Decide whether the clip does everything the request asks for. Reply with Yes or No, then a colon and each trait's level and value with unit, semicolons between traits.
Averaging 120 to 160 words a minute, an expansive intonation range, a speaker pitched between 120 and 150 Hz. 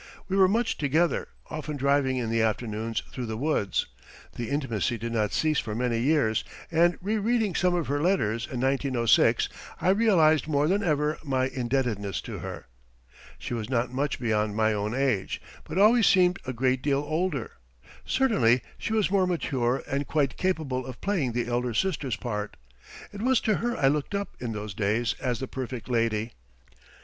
No: average, 180 wpm; wide, 6.3 semitones; low, 135 Hz